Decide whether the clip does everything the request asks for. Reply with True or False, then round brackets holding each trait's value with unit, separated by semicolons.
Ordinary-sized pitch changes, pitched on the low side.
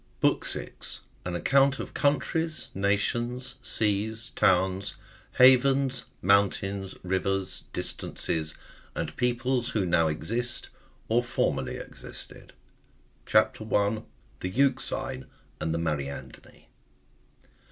True (4.9 semitones; 105 Hz)